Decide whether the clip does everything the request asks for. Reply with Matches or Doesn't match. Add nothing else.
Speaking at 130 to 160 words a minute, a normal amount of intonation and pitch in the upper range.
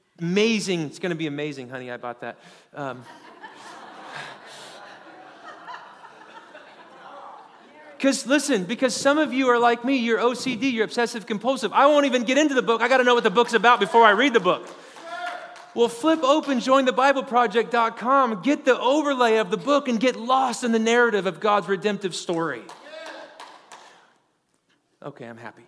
Matches